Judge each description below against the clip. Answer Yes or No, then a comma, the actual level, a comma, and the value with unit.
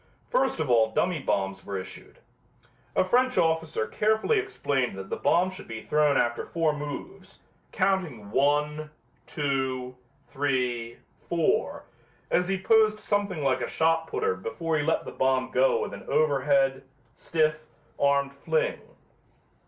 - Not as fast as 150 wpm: Yes, average, 140 wpm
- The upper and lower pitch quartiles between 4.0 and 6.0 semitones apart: Yes, wide, 5.4 semitones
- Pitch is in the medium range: Yes, medium, 150 Hz